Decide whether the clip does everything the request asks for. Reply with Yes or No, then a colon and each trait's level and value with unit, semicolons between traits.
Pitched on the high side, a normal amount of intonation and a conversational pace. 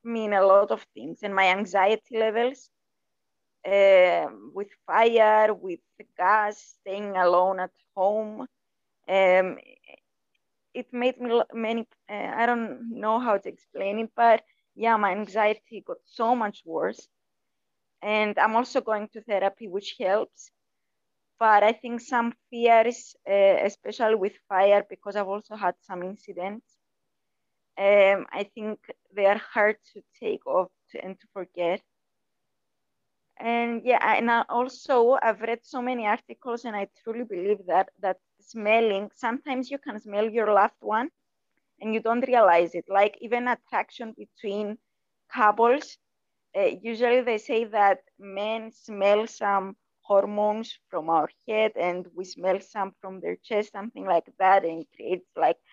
Yes: high, 215 Hz; average, 3.0 semitones; average, 145 wpm